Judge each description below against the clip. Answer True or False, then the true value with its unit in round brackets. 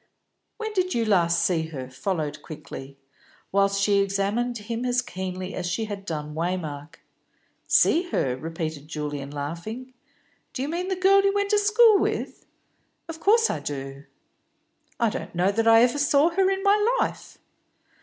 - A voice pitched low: False (200 Hz)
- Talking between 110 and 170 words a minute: True (165 wpm)